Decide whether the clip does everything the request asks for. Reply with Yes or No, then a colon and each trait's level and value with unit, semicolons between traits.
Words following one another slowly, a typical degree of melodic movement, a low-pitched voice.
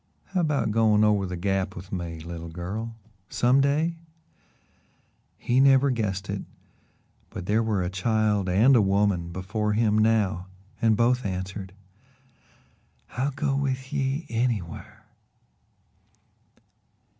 Yes: slow, 125 wpm; average, 4.9 semitones; low, 105 Hz